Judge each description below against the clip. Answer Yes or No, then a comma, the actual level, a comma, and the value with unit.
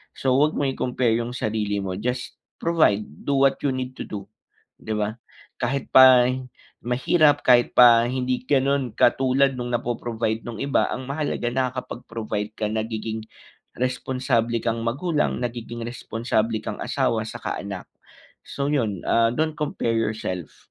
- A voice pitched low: Yes, low, 120 Hz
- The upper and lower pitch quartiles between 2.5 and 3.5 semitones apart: Yes, average, 2.8 semitones